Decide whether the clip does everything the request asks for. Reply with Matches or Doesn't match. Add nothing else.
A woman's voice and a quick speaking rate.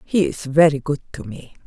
Matches